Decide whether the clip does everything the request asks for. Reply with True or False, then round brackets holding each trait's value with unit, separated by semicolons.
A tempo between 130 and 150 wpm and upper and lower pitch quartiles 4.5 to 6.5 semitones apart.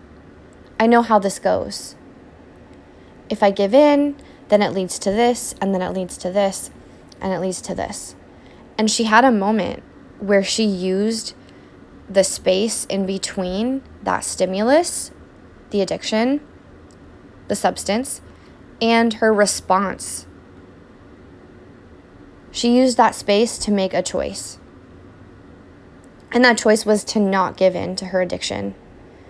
False (135 wpm; 3.6 semitones)